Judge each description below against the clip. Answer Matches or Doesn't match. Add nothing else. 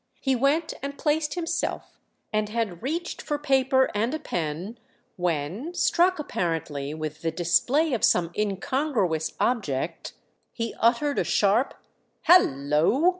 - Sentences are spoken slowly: Matches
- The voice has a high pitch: Matches